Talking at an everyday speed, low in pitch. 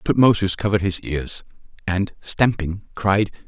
No: slow, 120 wpm; very low, 95 Hz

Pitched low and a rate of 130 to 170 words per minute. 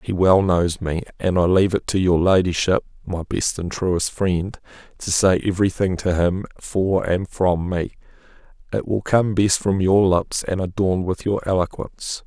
No: very low, 95 Hz; average, 185 wpm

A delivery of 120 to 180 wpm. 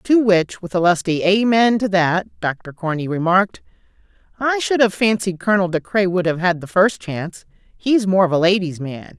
No: average, 195 wpm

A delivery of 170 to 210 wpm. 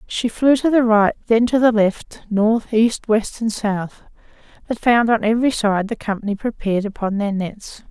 Yes: average, 190 wpm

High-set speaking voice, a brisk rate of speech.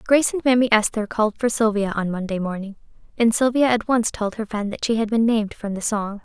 Yes: high, 220 Hz; fast, 240 wpm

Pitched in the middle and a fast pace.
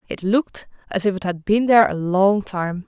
No: high, 200 Hz; fast, 230 wpm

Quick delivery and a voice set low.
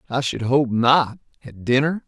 No: average, 145 wpm; low, 130 Hz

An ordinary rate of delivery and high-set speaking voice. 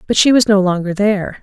No: fast, 255 wpm; high, 200 Hz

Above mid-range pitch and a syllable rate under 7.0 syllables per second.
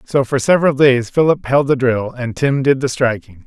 No: low, 130 Hz; 5.0 syllables/s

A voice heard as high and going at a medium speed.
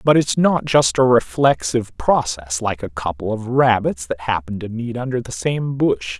No: low, 110 Hz; average, 195 wpm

